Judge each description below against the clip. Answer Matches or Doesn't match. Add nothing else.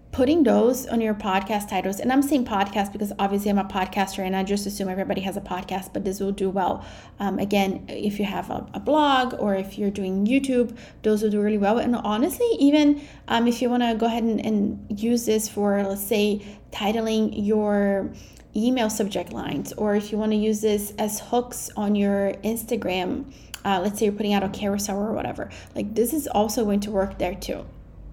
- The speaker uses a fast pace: Matches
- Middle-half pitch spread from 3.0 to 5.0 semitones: Doesn't match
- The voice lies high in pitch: Matches